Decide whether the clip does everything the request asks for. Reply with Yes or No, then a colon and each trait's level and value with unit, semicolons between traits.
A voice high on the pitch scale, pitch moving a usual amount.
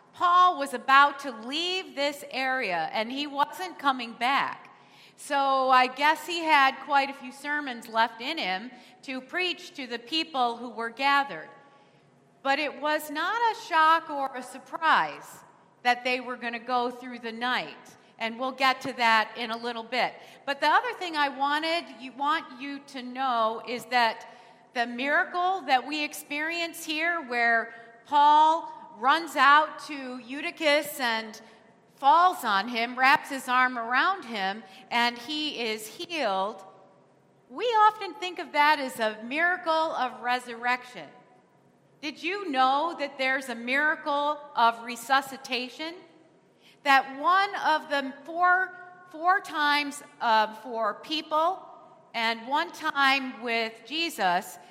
Yes: very high, 275 Hz; average, 4.4 semitones